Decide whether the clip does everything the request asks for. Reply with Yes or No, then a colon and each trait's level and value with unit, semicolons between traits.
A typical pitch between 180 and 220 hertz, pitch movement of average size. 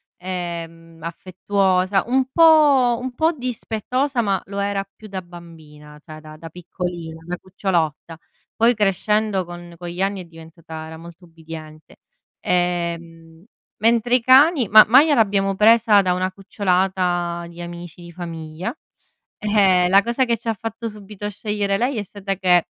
Yes: medium, 185 Hz; average, 4.0 semitones